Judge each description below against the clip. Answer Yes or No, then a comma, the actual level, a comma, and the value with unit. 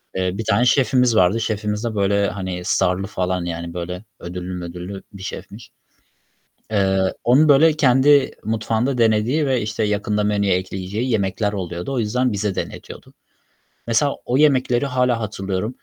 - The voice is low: Yes, low, 105 Hz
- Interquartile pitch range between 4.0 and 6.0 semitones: Yes, average, 4.7 semitones